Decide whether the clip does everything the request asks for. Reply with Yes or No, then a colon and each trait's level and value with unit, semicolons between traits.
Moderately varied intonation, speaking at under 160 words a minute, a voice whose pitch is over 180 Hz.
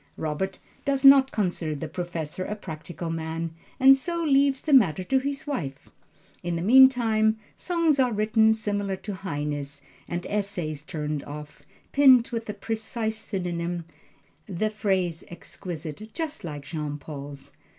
No: wide, 6.6 semitones; average, 140 wpm; high, 190 Hz